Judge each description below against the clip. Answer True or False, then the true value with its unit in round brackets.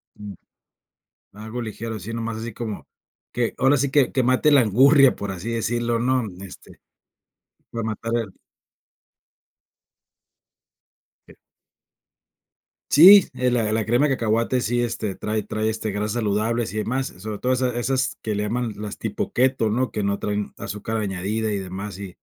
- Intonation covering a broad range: False (2.8 semitones)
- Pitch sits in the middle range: False (115 Hz)